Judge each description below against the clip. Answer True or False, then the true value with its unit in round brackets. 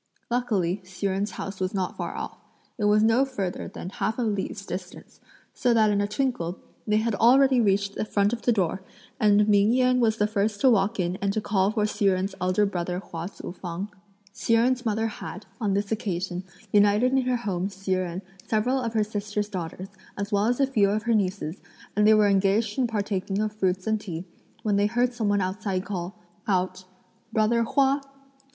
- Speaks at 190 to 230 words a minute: True (205 wpm)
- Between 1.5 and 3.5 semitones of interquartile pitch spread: True (2.6 semitones)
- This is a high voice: True (205 Hz)